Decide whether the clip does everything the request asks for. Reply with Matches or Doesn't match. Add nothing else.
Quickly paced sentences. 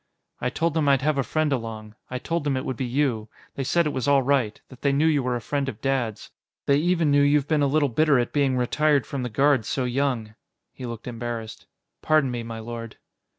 Matches